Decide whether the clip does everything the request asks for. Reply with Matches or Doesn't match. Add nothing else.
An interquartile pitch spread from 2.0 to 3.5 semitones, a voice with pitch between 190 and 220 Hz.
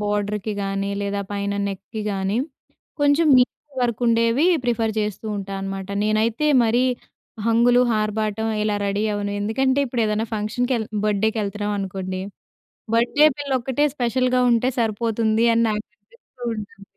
Matches